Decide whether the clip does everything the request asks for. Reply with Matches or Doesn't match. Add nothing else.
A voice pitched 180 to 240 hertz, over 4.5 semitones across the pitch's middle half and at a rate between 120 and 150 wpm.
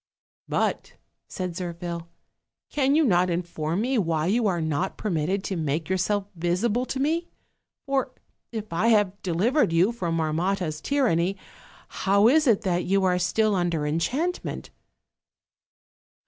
Matches